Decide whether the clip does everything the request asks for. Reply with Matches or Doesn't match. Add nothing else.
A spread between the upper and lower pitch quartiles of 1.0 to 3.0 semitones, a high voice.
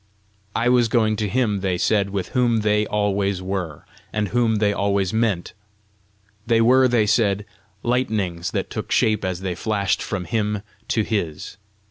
Doesn't match